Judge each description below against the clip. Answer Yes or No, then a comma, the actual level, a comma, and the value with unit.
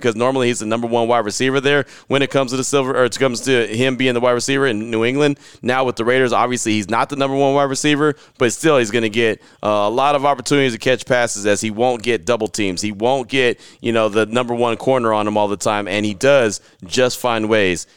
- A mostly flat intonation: No, average, 3.3 semitones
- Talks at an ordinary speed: No, fast, 255 wpm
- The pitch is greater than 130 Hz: No, low, 125 Hz